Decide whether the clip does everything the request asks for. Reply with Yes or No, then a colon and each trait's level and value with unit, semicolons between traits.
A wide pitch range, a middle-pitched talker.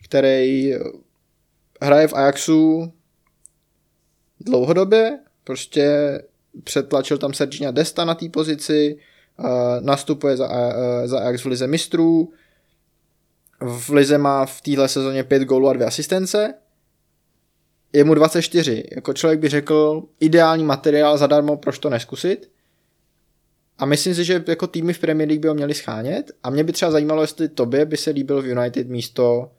No: average, 2.9 semitones; medium, 150 Hz